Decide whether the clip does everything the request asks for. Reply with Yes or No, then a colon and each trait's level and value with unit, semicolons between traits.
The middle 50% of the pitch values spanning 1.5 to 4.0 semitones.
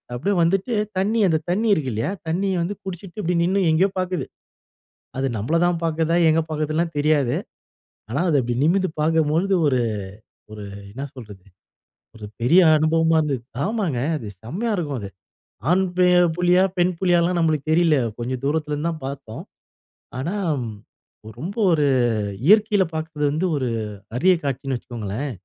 No: average, 4.6 semitones